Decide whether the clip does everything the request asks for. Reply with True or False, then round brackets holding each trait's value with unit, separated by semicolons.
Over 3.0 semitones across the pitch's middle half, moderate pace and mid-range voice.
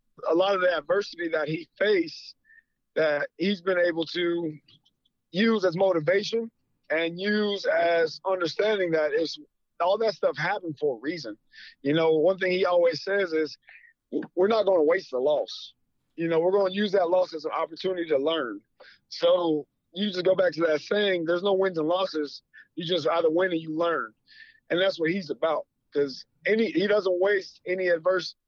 True (3.8 semitones; 190 wpm; 180 Hz)